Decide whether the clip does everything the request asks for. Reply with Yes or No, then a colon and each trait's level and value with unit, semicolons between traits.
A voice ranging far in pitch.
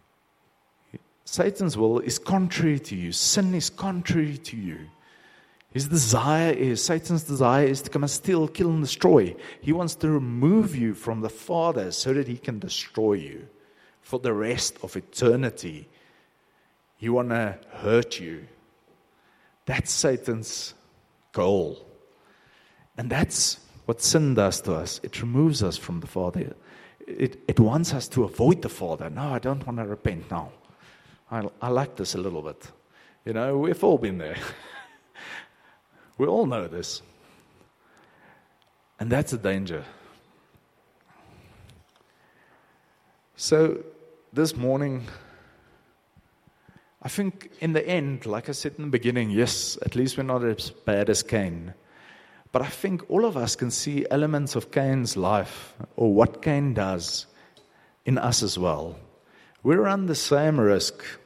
Yes: wide, 5.7 semitones